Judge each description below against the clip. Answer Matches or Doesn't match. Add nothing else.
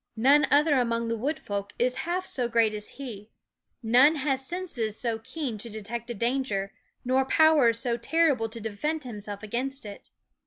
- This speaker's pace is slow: Doesn't match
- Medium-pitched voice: Doesn't match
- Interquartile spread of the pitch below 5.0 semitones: Matches